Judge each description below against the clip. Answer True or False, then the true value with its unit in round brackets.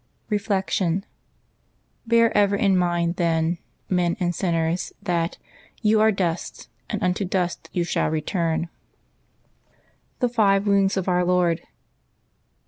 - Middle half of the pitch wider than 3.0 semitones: False (2.7 semitones)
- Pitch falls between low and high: True (180 Hz)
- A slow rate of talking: True (125 wpm)